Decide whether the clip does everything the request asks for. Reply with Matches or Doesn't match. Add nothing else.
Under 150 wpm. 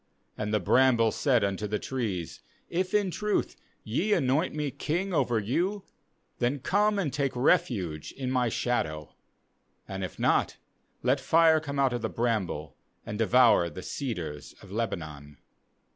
Doesn't match